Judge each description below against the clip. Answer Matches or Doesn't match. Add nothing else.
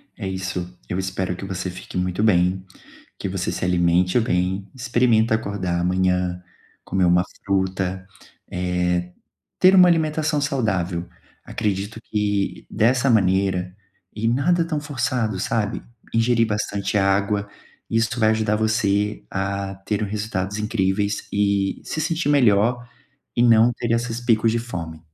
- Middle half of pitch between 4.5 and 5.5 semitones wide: Doesn't match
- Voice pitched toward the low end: Matches